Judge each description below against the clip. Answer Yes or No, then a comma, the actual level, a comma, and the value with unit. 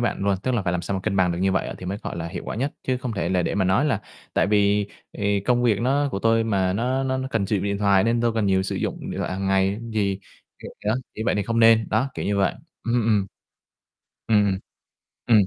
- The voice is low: Yes, low, 105 Hz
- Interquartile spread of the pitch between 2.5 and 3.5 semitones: Yes, average, 3.0 semitones